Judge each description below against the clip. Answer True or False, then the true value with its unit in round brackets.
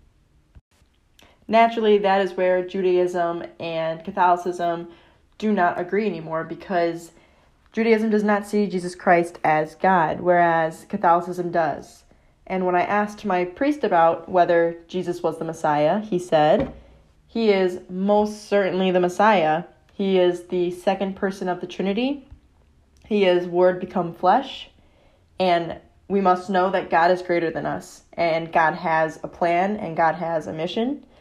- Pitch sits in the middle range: True (180 Hz)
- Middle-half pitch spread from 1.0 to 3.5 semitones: True (2.7 semitones)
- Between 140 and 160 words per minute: True (145 wpm)